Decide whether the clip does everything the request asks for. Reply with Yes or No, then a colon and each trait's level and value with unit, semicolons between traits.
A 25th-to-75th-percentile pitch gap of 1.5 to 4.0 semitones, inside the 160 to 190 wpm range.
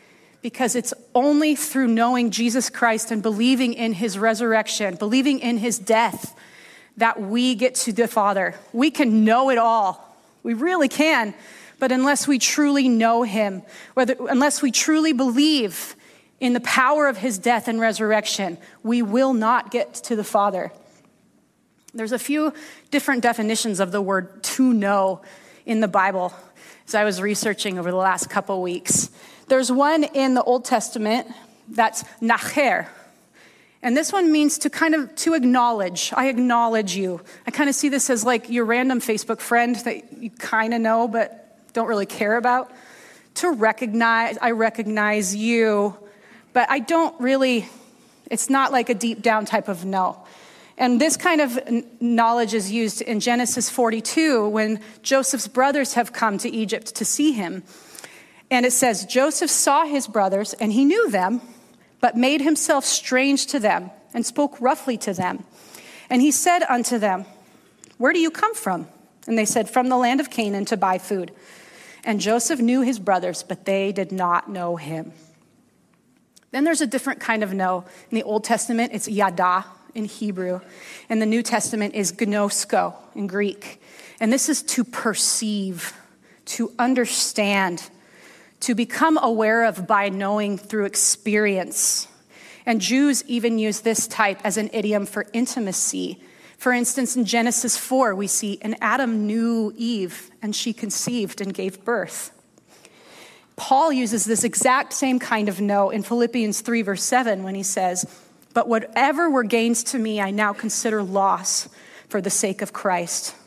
Yes: average, 3.4 semitones; average, 165 wpm